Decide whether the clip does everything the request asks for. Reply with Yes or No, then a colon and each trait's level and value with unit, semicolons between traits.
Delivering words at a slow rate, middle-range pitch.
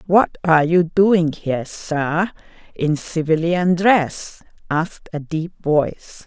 Yes: slow, 125 wpm; medium, 165 Hz